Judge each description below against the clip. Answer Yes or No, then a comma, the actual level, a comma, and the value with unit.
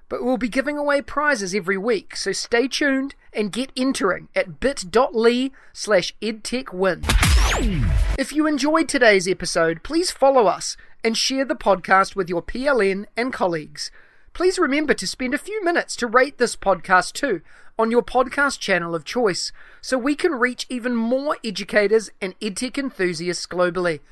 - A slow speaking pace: No, average, 155 wpm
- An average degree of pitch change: No, wide, 6.1 semitones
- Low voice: No, high, 240 Hz